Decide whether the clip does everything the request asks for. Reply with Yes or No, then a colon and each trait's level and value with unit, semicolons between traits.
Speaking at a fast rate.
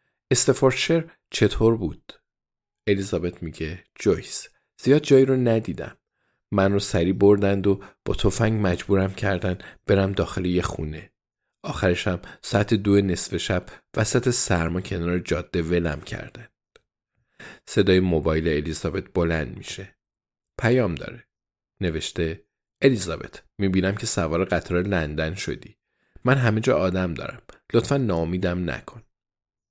No: average, 115 wpm